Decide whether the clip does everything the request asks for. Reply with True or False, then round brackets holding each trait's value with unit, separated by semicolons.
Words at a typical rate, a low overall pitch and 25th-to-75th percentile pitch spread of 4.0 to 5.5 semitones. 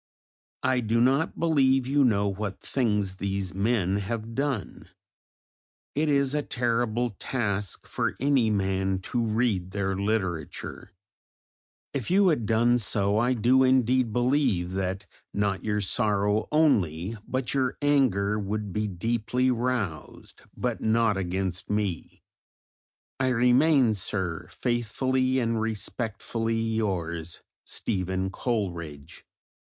False (115 wpm; 110 Hz; 4.4 semitones)